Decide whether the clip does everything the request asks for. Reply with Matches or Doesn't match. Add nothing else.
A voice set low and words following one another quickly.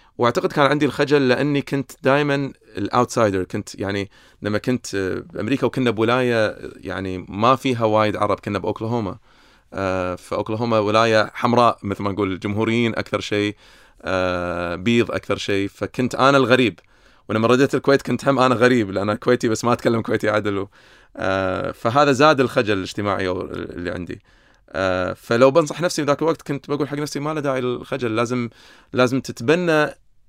Matches